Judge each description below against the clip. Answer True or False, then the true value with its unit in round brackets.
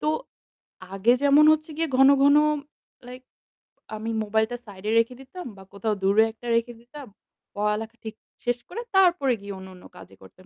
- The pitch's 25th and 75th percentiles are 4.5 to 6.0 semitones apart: True (4.9 semitones)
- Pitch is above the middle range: True (230 Hz)